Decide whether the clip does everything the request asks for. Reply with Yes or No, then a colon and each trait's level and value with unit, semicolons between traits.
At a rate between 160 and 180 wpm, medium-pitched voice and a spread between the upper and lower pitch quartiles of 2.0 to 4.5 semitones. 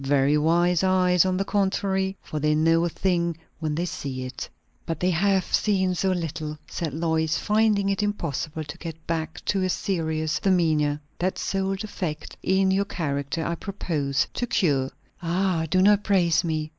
Yes: average, 170 wpm; medium, 170 Hz; average, 3.5 semitones